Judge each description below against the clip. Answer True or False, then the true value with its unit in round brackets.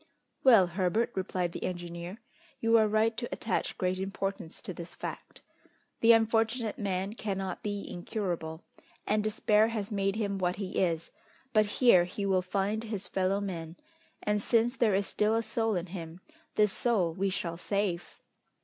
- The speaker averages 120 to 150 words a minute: False (165 wpm)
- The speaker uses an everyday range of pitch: True (3.0 semitones)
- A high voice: True (200 Hz)